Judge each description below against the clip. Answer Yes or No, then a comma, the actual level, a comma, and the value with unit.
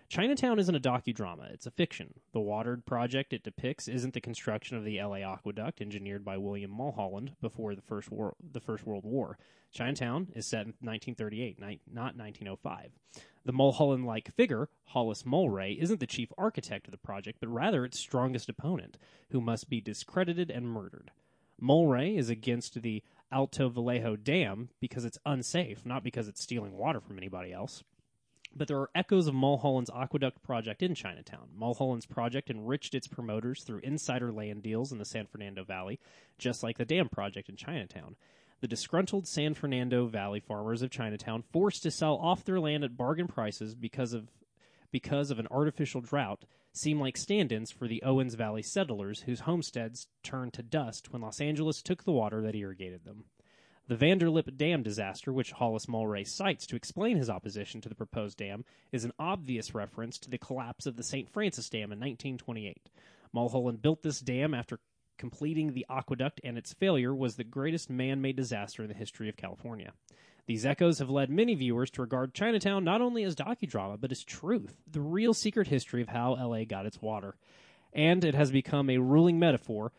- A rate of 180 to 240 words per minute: Yes, average, 185 wpm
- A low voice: Yes, low, 125 Hz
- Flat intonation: No, average, 4.9 semitones